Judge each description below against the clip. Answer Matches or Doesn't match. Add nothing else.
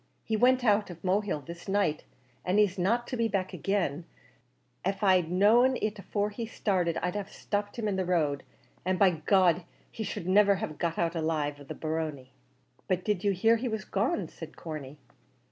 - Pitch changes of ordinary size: Matches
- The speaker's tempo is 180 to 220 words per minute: Matches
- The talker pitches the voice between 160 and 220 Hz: Matches